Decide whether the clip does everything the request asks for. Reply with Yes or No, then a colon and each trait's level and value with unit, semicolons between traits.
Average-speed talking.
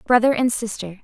Yes: average, 175 wpm